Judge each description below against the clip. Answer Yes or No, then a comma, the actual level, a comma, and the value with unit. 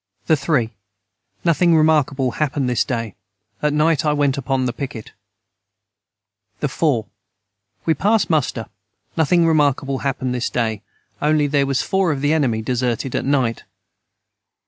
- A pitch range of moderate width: Yes, average, 3.7 semitones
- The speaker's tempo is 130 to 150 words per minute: Yes, average, 140 wpm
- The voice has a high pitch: No, medium, 140 Hz